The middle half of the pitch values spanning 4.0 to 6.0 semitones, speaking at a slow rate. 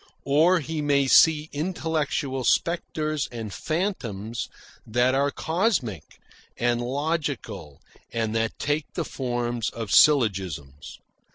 Yes: average, 5.3 semitones; slow, 105 wpm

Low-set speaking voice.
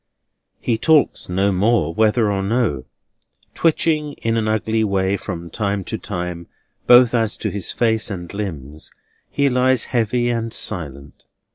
Yes: low, 110 Hz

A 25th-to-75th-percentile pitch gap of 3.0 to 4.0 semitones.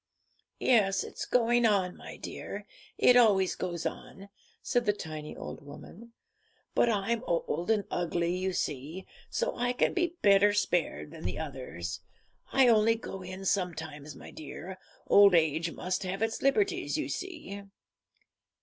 No: wide, 5.5 semitones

